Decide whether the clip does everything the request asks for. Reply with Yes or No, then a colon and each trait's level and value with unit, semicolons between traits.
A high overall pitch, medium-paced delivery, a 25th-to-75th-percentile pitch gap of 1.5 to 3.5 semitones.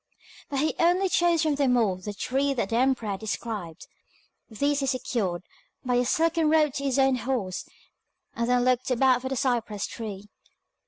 No: very high, 255 Hz; average, 180 wpm; average, 4.1 semitones